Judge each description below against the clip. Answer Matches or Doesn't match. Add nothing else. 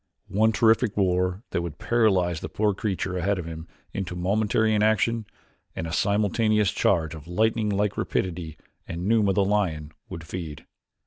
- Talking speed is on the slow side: Doesn't match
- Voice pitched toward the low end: Matches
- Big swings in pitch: Doesn't match